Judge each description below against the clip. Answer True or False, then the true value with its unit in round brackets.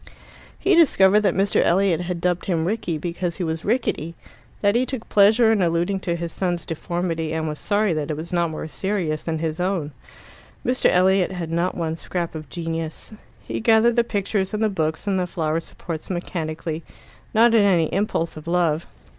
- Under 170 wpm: False (190 wpm)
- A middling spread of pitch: True (3.6 semitones)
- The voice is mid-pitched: True (175 Hz)